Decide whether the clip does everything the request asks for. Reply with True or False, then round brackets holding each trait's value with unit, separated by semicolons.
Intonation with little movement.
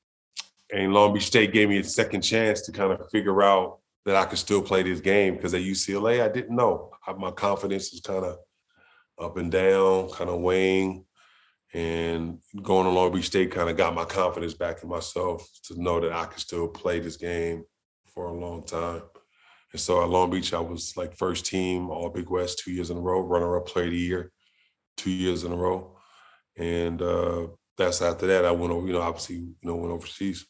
True (1.9 semitones)